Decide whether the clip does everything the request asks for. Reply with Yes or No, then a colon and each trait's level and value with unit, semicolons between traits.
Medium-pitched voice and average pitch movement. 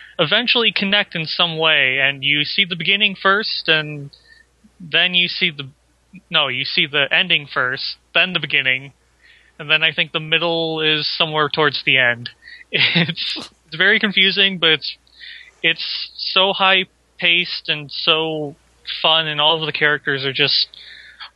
Yes: medium, 165 Hz; average, 4.0 semitones